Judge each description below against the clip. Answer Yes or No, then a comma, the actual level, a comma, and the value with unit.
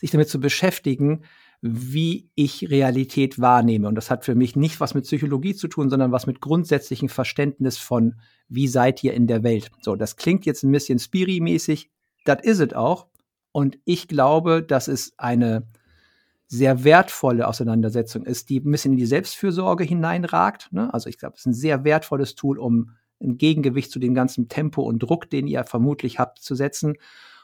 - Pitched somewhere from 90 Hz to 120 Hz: No, low, 135 Hz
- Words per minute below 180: No, average, 185 wpm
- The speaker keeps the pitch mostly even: No, average, 3.6 semitones